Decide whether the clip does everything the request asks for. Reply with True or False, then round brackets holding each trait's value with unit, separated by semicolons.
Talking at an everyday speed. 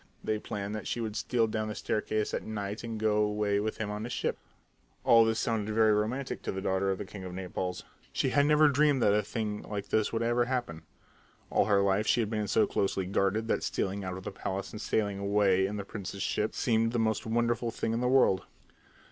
False (230 wpm)